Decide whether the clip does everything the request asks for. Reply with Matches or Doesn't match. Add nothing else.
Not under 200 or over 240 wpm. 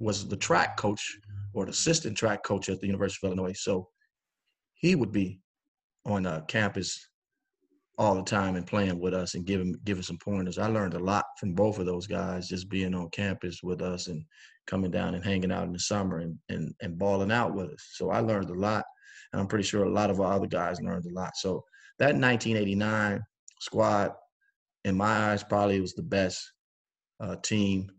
Matches